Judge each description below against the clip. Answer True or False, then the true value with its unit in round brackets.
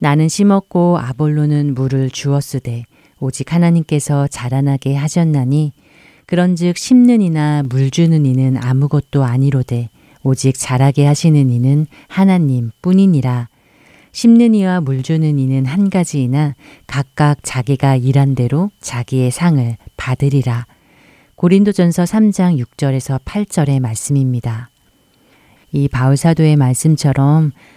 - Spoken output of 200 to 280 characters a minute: True (270 characters per minute)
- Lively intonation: False (3.7 semitones)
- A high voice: False (140 Hz)